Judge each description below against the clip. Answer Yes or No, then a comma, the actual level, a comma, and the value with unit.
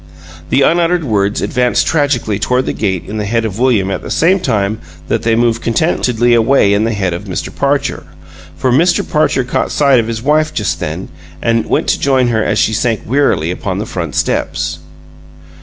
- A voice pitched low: Yes, low, 115 Hz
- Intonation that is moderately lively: Yes, average, 4.4 semitones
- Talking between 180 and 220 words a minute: Yes, average, 195 wpm